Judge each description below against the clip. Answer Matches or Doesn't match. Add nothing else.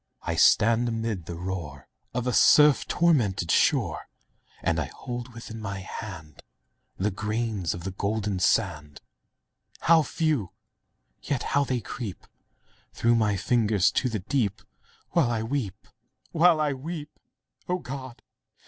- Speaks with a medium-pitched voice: Doesn't match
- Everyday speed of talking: Doesn't match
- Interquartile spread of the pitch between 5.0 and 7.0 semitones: Matches